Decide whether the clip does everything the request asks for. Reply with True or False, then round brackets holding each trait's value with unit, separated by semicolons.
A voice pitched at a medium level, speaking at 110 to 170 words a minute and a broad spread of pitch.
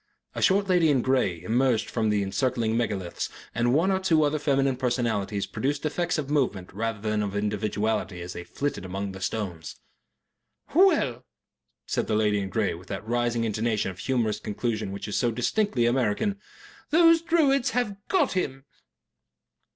False (120 Hz; 165 wpm; 6.0 semitones)